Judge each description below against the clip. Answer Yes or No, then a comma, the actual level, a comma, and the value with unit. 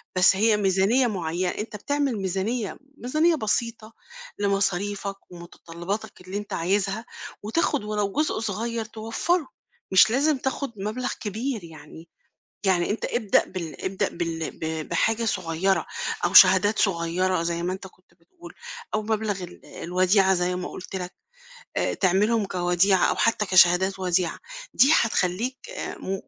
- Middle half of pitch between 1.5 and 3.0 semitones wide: No, average, 3.6 semitones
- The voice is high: Yes, high, 195 Hz